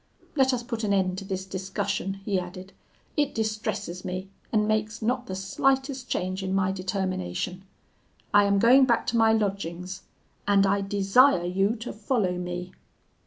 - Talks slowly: No, average, 165 wpm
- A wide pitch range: No, average, 3.1 semitones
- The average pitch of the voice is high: Yes, high, 195 Hz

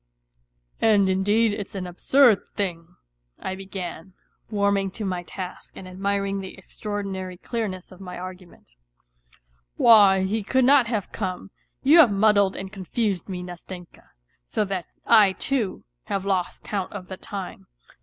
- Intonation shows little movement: Yes, narrow, 2.1 semitones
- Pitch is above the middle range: Yes, high, 195 Hz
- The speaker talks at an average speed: Yes, average, 150 wpm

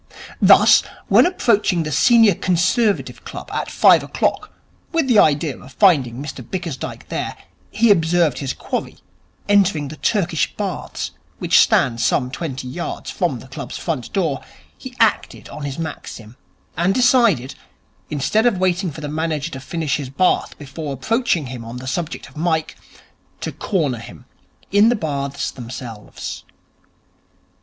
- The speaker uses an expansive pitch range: Yes, wide, 6.4 semitones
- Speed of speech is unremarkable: Yes, average, 150 wpm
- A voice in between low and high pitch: Yes, medium, 160 Hz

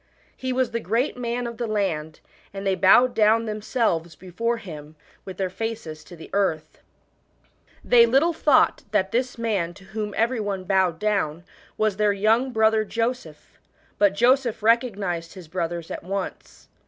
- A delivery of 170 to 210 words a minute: No, average, 160 wpm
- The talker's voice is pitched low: No, high, 210 Hz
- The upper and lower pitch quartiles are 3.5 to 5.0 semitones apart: Yes, average, 4.0 semitones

